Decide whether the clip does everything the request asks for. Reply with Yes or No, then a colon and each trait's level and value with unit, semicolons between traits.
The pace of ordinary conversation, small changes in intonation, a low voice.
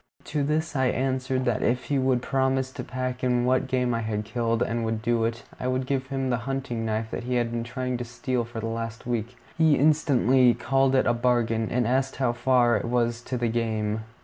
No: fast, 230 wpm; narrow, 2.1 semitones; low, 125 Hz